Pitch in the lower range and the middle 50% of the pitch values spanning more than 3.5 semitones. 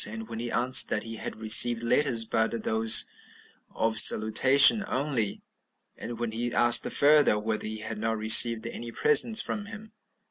No: low, 115 Hz; average, 2.7 semitones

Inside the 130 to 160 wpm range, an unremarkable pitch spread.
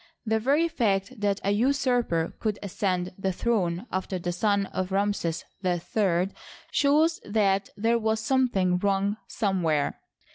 Yes: slow, 135 wpm; average, 3.6 semitones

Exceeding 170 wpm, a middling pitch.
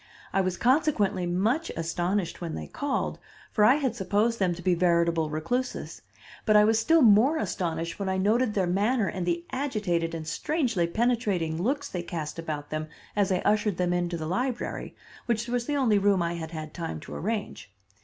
No: average, 190 wpm; high, 195 Hz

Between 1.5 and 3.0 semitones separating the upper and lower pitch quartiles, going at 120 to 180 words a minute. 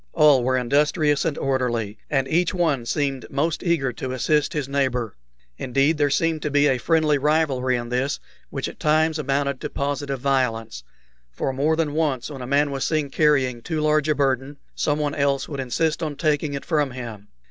No: average, 2.7 semitones; average, 190 wpm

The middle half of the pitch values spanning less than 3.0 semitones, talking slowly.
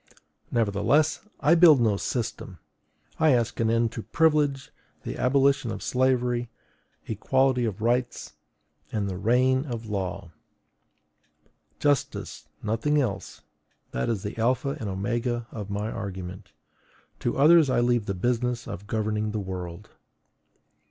No: average, 4.0 semitones; slow, 130 wpm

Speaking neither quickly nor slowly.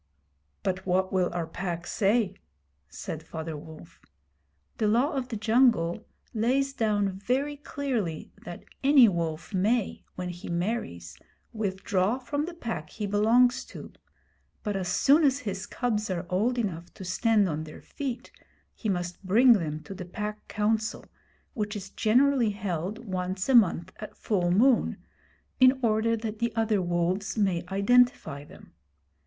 Yes: average, 150 wpm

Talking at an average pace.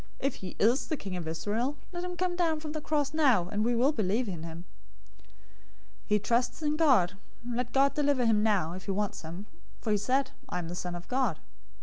No: fast, 225 wpm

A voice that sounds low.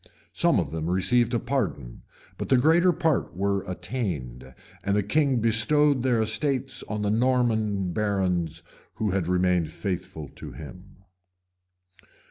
Yes: low, 105 Hz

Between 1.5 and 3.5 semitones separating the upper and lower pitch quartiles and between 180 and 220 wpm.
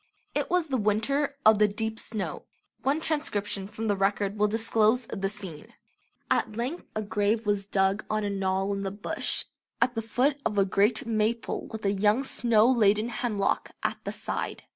Yes: narrow, 2.5 semitones; average, 185 wpm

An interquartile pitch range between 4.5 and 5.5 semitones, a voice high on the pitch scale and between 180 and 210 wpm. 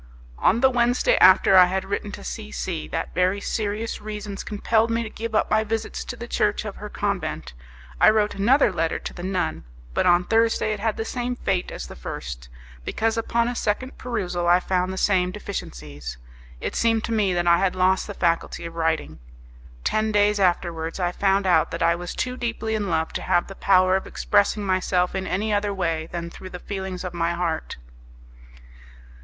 No: average, 3.7 semitones; high, 195 Hz; average, 200 wpm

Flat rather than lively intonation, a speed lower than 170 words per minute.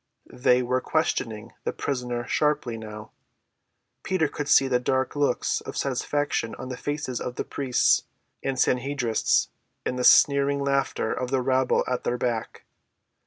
Yes: narrow, 2.3 semitones; average, 150 wpm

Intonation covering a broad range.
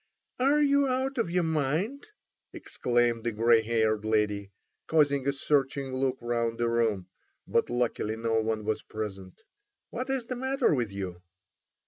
Yes: wide, 7.4 semitones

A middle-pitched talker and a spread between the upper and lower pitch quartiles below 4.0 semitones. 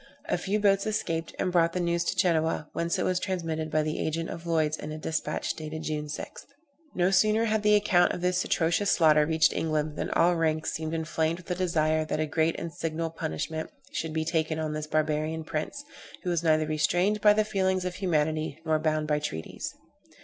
Yes: medium, 160 Hz; narrow, 2.4 semitones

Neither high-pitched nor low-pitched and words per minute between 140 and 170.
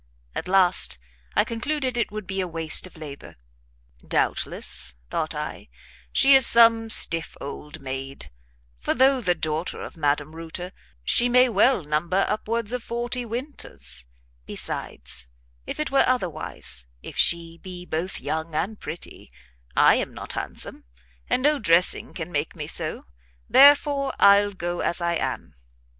Yes: medium, 180 Hz; average, 150 wpm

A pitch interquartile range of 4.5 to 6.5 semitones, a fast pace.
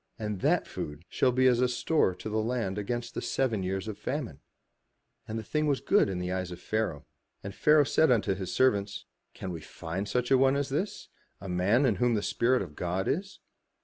Yes: wide, 5.4 semitones; fast, 215 wpm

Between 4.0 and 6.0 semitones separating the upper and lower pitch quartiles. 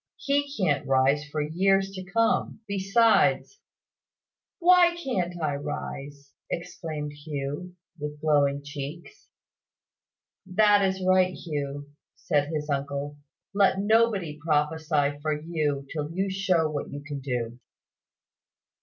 Yes: average, 5.0 semitones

